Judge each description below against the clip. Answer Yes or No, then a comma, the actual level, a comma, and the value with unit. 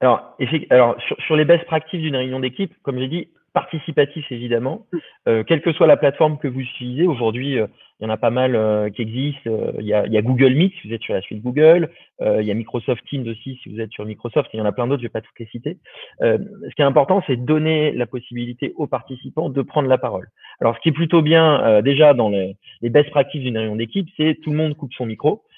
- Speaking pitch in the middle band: No, low, 130 Hz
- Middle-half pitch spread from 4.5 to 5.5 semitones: Yes, average, 4.8 semitones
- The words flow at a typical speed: No, fast, 265 wpm